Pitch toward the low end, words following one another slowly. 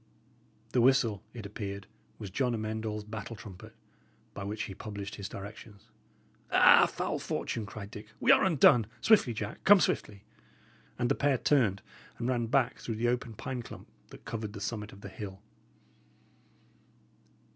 No: low, 110 Hz; average, 160 wpm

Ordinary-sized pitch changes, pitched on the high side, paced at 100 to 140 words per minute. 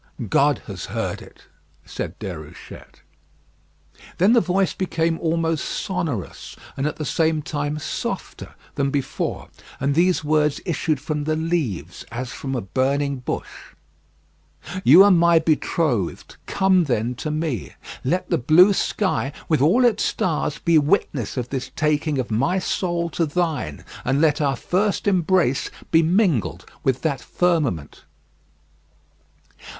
No: average, 4.1 semitones; medium, 155 Hz; slow, 135 wpm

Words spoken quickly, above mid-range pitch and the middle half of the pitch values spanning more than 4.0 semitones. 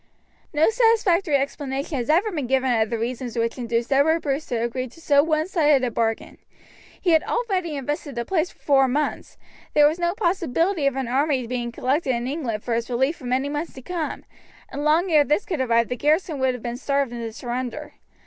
Yes: fast, 210 wpm; very high, 280 Hz; average, 4.4 semitones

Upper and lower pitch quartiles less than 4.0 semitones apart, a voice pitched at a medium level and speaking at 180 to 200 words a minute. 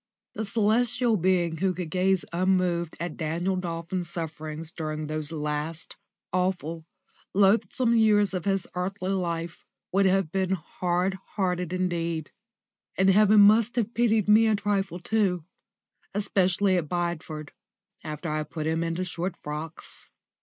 No: average, 3.0 semitones; medium, 180 Hz; average, 140 wpm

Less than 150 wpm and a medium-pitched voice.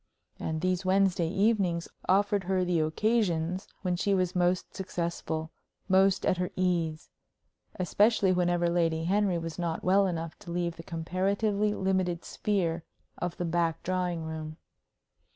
Yes: average, 140 wpm; medium, 180 Hz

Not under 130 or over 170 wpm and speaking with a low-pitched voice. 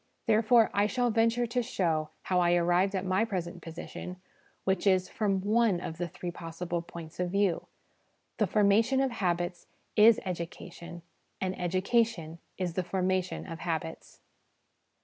No: average, 150 wpm; medium, 185 Hz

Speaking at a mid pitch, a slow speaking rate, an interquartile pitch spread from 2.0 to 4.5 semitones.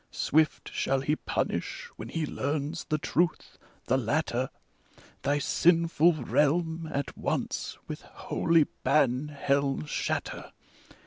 Yes: medium, 150 Hz; slow, 120 wpm; average, 2.9 semitones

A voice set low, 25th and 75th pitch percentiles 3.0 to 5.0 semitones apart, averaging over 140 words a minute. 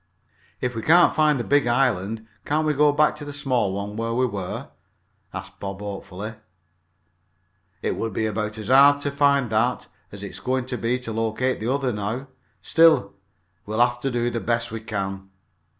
Yes: low, 120 Hz; average, 4.2 semitones; average, 185 wpm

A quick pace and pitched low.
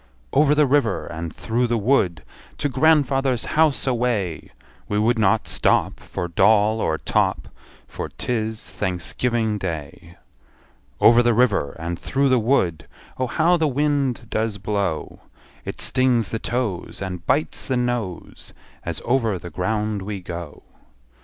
No: average, 145 wpm; low, 110 Hz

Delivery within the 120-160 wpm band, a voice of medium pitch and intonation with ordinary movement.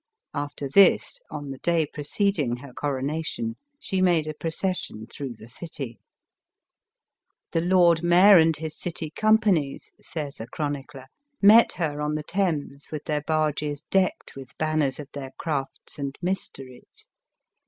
Yes: average, 145 wpm; medium, 155 Hz; average, 3.8 semitones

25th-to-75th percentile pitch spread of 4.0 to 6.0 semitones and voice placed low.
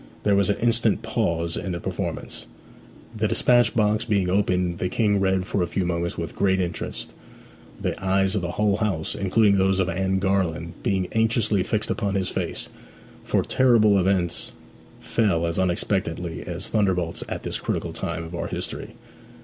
No: average, 2.8 semitones; very low, 95 Hz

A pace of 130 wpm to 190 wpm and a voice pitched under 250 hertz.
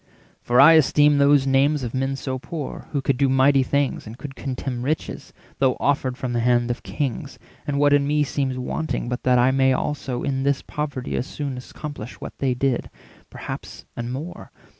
No: average, 200 wpm; low, 135 Hz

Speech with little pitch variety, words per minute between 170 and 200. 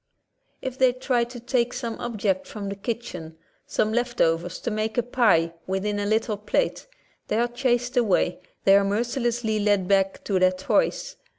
No: average, 3.6 semitones; average, 180 wpm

